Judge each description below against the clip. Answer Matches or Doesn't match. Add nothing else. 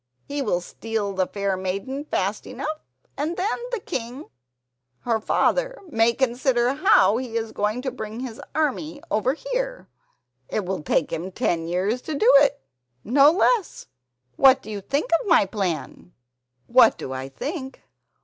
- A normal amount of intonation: Doesn't match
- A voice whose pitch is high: Matches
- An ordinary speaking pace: Matches